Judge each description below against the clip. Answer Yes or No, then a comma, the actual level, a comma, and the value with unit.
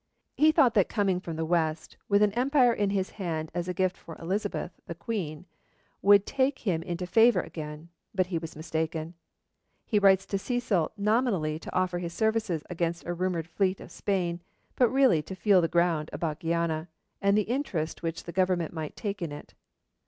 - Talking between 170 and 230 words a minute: Yes, average, 190 wpm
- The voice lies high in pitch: No, medium, 180 Hz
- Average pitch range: Yes, average, 3.7 semitones